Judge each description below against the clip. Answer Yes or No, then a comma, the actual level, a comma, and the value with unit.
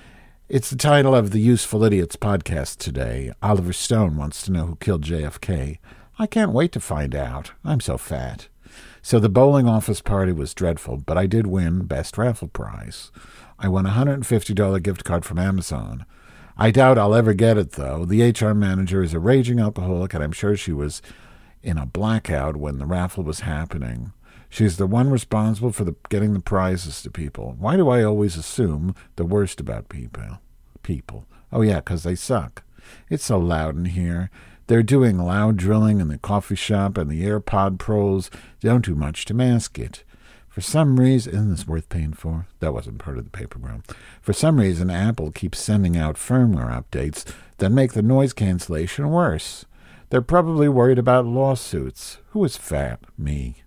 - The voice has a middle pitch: No, low, 100 Hz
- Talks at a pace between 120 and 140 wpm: No, average, 185 wpm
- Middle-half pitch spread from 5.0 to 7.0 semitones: Yes, wide, 5.5 semitones